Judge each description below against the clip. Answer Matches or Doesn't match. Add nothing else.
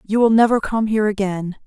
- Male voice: Doesn't match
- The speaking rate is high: Matches